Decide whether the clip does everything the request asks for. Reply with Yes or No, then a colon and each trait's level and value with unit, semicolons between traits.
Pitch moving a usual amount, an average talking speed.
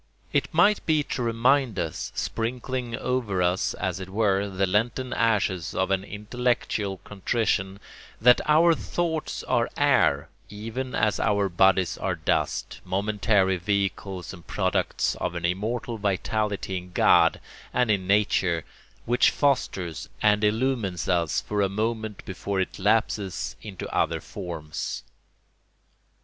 No: average, 3.8 semitones; slow, 130 wpm